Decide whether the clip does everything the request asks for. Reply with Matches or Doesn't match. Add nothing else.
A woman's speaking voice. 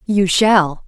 Matches